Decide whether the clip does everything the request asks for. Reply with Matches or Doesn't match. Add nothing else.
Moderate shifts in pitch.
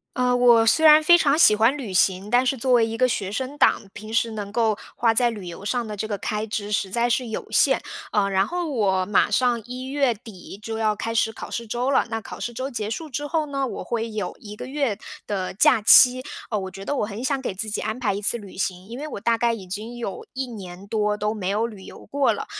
Matches